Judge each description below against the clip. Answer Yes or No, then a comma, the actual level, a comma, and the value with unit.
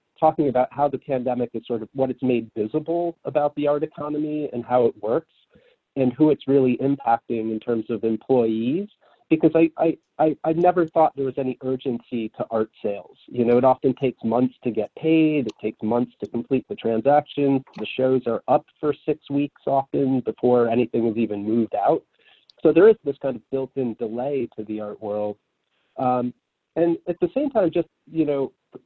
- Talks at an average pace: Yes, average, 195 wpm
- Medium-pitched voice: No, low, 130 Hz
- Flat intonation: No, average, 4.1 semitones